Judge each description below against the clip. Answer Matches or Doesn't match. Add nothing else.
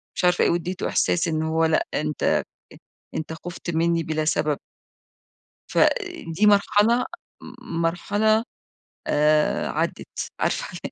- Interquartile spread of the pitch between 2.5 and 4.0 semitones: Matches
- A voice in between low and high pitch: Matches